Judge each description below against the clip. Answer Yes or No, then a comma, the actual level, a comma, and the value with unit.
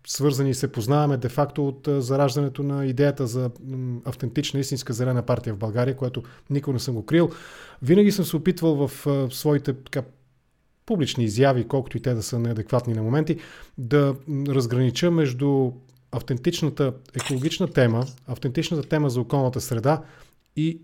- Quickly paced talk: No, average, 145 wpm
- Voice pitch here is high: No, low, 135 Hz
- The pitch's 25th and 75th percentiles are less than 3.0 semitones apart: Yes, narrow, 2.5 semitones